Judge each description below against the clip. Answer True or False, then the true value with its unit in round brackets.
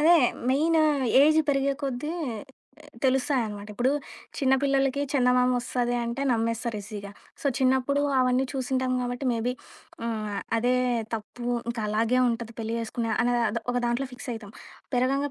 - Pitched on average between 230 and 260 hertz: True (250 Hz)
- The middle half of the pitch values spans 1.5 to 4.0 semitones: True (2.6 semitones)